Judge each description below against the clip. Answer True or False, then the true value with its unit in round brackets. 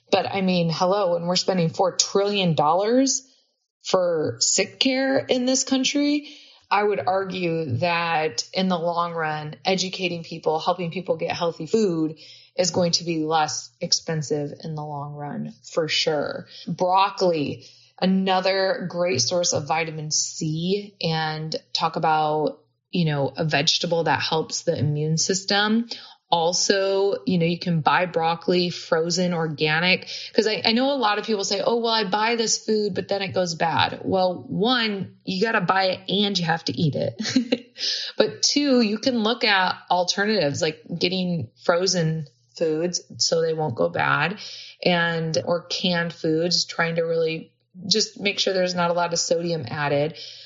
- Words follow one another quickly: False (165 wpm)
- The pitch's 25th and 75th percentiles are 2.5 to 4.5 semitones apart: True (3.8 semitones)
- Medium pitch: True (175 Hz)